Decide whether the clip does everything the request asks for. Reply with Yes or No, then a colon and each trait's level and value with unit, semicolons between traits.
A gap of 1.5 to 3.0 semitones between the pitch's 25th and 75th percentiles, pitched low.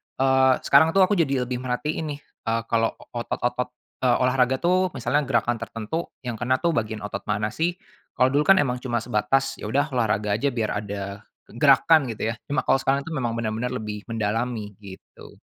No: average, 3.7 semitones; low, 125 Hz